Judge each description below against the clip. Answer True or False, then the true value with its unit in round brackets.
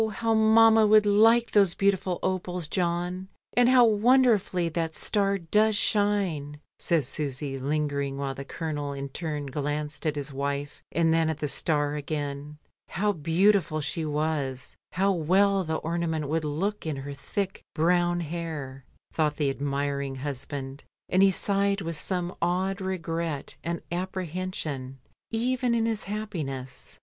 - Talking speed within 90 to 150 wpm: True (145 wpm)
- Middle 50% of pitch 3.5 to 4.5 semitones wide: False (5.1 semitones)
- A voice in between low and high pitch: True (165 Hz)